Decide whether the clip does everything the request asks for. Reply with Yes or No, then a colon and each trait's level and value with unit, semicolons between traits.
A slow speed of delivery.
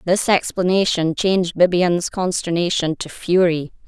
Yes: slow, 110 wpm